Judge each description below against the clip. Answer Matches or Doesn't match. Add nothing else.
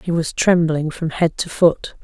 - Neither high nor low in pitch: Matches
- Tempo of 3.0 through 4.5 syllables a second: Matches